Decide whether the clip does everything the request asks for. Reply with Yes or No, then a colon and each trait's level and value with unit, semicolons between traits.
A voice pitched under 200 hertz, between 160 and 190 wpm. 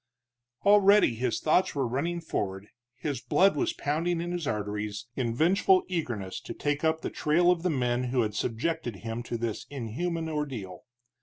Yes: medium, 140 Hz; average, 170 wpm